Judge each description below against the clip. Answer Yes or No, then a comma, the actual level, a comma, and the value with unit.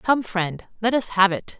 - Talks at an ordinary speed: No, fast, 225 wpm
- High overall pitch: Yes, high, 205 Hz